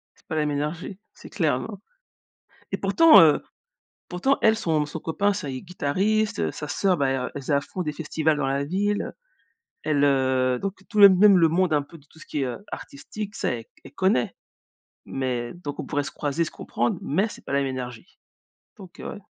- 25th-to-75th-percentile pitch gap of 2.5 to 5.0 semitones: No, wide, 5.4 semitones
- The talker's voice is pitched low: No, medium, 155 Hz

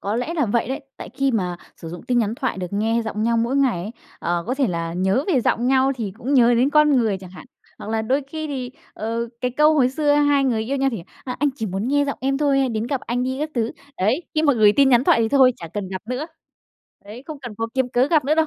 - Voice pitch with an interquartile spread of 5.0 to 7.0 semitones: No, average, 4.0 semitones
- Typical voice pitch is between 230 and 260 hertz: Yes, very high, 250 Hz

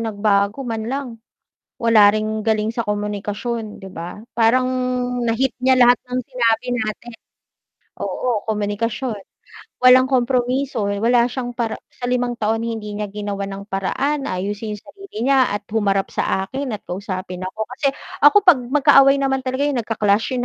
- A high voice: Yes, high, 230 Hz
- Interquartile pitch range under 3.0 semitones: No, average, 3.6 semitones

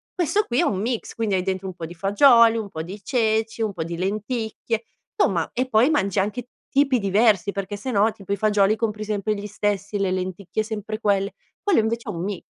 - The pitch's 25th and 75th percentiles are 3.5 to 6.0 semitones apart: No, narrow, 2.5 semitones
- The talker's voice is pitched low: No, high, 210 Hz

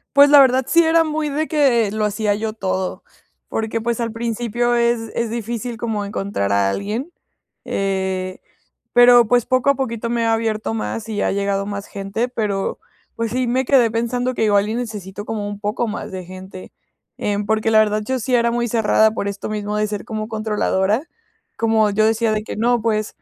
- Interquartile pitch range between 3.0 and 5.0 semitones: No, narrow, 2.6 semitones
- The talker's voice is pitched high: Yes, high, 220 Hz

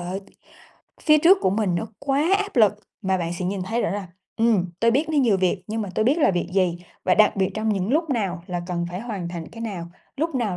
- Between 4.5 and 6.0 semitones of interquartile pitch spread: Yes, average, 4.8 semitones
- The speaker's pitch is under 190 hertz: No, high, 205 Hz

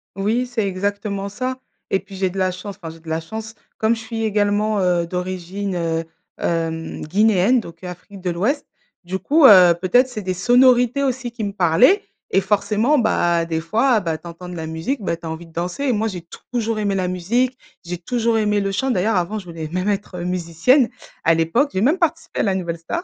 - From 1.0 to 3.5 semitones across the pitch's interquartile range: No, average, 4.6 semitones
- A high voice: Yes, high, 195 Hz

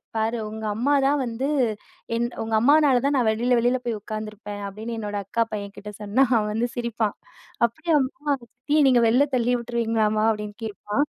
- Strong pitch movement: No, average, 2.8 semitones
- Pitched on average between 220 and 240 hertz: Yes, high, 230 Hz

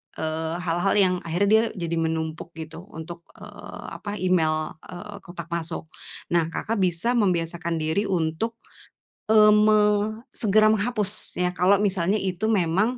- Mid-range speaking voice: Yes, medium, 180 Hz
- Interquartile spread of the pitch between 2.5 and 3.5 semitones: No, average, 4.0 semitones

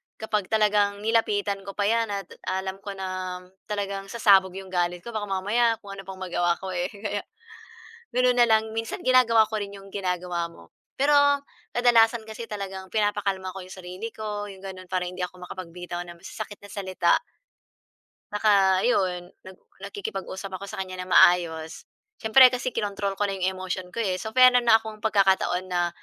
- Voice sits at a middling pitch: No, high, 195 Hz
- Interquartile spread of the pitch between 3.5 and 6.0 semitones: No, average, 2.8 semitones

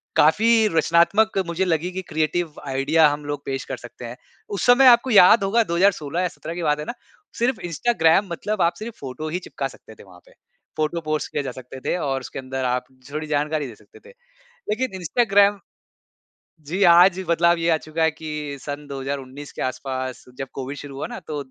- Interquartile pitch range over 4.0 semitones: Yes, average, 4.6 semitones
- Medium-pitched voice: Yes, medium, 155 Hz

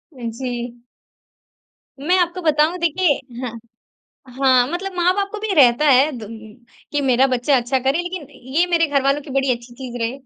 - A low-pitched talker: No, very high, 275 Hz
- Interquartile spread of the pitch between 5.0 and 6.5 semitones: Yes, wide, 5.4 semitones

